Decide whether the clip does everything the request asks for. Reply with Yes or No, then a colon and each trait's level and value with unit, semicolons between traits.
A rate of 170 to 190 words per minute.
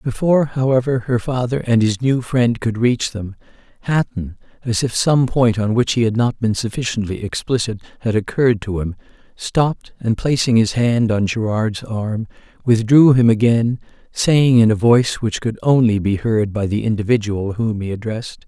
Yes: average, 175 wpm